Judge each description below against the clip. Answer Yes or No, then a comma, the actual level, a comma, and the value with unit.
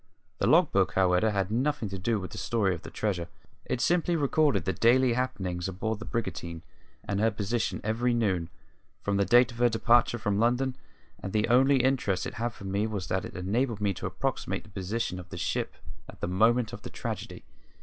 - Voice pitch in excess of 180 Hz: No, low, 110 Hz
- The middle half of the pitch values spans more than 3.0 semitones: Yes, average, 4.1 semitones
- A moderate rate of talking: No, fast, 210 wpm